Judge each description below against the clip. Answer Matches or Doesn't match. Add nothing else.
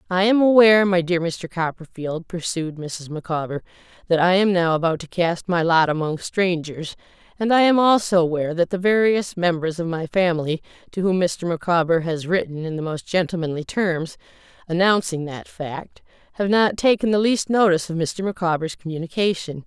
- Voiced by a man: Doesn't match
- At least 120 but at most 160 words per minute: Doesn't match